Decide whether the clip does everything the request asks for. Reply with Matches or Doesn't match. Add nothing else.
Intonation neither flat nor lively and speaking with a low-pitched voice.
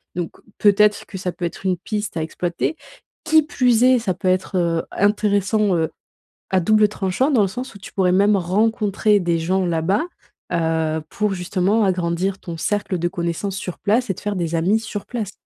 Doesn't match